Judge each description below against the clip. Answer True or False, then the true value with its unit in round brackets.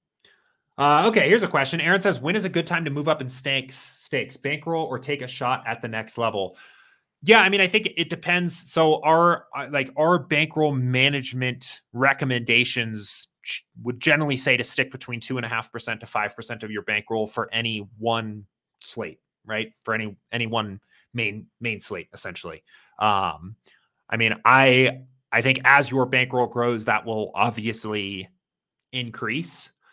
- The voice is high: False (125 Hz)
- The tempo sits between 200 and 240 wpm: False (160 wpm)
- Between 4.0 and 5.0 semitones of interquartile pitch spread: True (4.3 semitones)